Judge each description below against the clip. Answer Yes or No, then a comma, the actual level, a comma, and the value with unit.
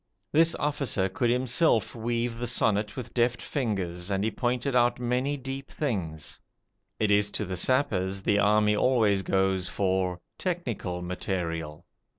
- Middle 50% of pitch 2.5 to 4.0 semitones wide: No, average, 4.8 semitones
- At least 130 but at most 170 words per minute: Yes, average, 145 wpm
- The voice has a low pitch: Yes, low, 105 Hz